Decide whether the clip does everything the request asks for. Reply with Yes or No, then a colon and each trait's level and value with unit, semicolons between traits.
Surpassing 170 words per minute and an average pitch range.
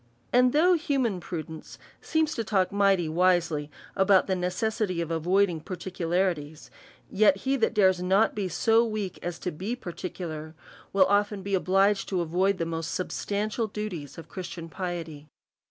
No: average, 160 wpm; average, 3.5 semitones